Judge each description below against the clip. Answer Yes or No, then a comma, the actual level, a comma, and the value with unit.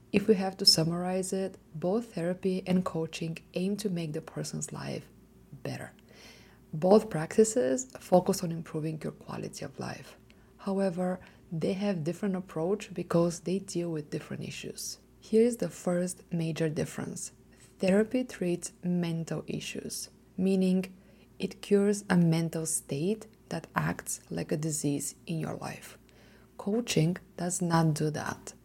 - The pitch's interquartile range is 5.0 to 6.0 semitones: No, average, 3.3 semitones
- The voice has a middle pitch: Yes, medium, 180 Hz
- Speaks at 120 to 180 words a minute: Yes, average, 140 wpm